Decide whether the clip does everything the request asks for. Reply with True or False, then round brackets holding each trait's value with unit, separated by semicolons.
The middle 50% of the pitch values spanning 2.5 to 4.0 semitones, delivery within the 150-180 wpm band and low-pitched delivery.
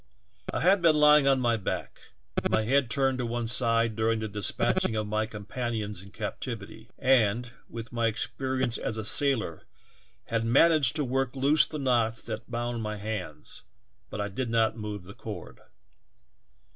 True (3.3 semitones; 170 wpm; 115 Hz)